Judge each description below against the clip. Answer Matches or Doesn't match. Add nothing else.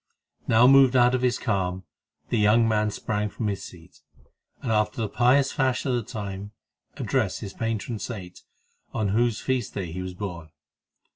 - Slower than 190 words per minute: Matches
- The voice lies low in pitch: Matches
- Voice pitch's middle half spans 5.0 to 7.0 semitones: Doesn't match